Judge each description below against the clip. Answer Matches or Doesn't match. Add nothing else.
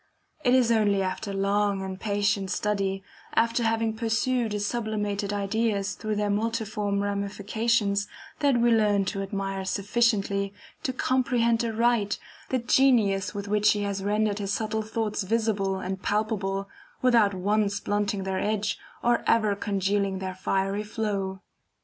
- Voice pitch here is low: Doesn't match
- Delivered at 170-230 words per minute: Doesn't match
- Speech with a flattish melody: Matches